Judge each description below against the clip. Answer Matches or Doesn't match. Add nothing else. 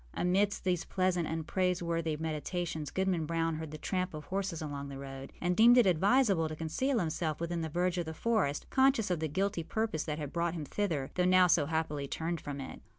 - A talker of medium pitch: Matches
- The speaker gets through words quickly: Matches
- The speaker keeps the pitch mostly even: Doesn't match